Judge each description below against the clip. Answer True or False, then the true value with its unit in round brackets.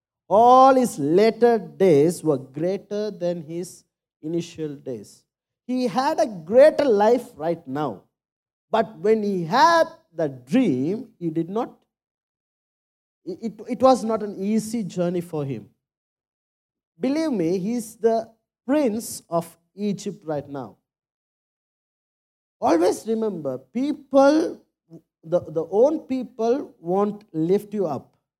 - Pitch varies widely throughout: True (6.6 semitones)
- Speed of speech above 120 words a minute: False (115 wpm)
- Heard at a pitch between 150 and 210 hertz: True (205 Hz)